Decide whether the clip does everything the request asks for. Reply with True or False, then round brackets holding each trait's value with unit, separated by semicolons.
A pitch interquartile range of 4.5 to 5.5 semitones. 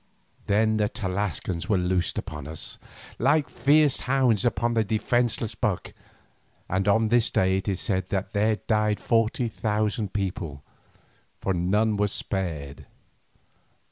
False (3.3 semitones)